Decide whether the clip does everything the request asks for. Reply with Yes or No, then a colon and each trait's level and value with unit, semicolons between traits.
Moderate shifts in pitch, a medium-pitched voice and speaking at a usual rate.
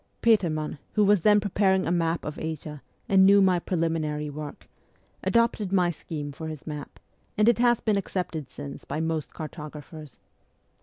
Yes: average, 4.5 semitones; medium, 165 Hz; average, 160 wpm